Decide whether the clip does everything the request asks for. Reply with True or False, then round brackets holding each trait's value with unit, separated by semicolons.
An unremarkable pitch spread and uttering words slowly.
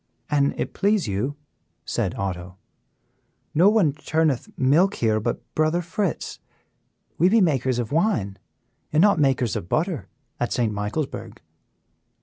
False (7.0 semitones; 130 wpm)